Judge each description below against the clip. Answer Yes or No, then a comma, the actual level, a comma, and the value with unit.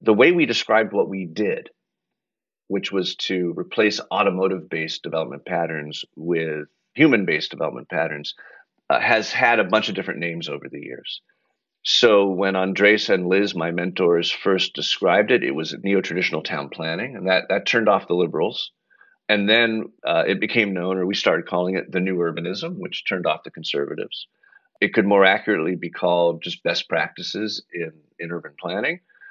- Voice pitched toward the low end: Yes, very low, 95 Hz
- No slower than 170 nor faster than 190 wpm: Yes, average, 175 wpm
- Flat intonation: No, average, 3.2 semitones